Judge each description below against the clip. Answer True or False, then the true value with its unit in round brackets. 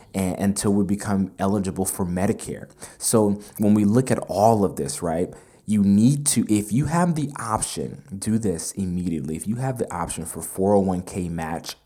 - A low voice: True (100 Hz)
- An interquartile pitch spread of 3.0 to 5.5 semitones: False (2.6 semitones)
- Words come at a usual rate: True (170 wpm)